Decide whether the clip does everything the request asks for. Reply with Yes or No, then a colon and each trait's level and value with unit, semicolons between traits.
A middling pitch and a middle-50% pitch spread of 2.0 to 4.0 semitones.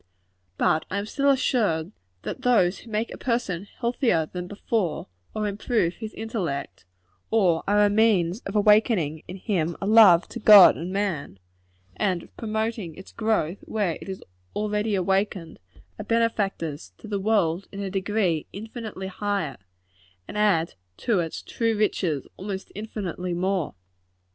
No: high, 200 Hz; average, 3.7 semitones